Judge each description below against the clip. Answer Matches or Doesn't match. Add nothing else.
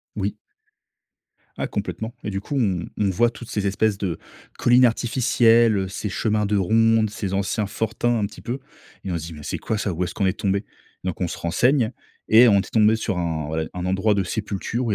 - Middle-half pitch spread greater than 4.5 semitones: Doesn't match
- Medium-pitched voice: Doesn't match